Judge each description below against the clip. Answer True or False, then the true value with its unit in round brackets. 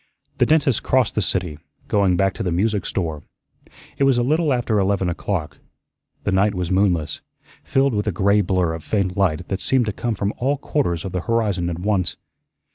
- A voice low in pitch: True (100 Hz)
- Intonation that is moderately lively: True (4.2 semitones)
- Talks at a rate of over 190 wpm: True (200 wpm)